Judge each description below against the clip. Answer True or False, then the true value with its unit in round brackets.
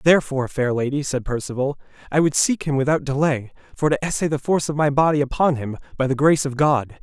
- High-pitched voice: False (140 Hz)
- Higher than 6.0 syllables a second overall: True (6.4 syllables/s)